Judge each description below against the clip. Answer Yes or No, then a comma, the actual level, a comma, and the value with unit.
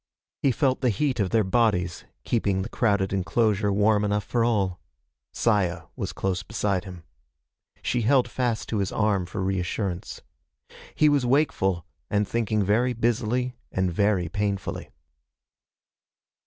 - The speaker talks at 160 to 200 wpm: No, average, 140 wpm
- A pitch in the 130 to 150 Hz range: No, low, 105 Hz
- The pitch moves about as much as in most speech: Yes, average, 3.6 semitones